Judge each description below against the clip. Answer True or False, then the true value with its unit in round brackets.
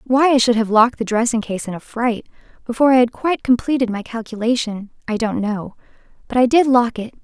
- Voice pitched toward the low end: False (235 Hz)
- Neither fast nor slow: False (215 wpm)